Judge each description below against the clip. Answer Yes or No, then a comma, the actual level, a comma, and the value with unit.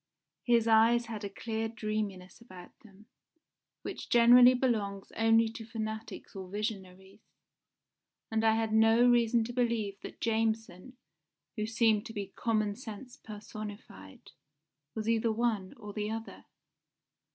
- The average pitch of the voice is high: Yes, high, 220 Hz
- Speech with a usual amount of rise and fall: No, narrow, 1.9 semitones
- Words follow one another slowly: Yes, slow, 130 wpm